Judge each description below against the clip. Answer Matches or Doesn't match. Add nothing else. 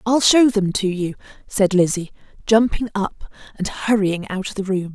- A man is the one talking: Doesn't match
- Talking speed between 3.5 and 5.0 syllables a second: Matches